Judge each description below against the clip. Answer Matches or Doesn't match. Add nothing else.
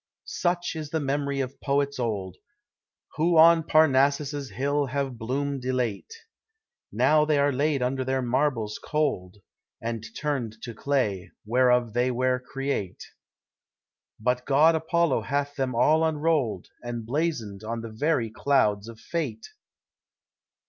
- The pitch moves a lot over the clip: Doesn't match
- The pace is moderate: Doesn't match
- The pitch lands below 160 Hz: Matches